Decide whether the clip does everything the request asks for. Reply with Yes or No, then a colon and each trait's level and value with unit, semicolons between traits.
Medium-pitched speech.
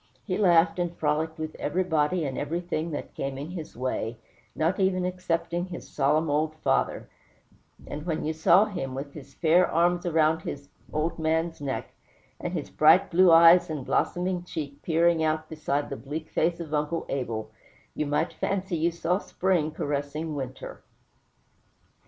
Yes: medium, 160 Hz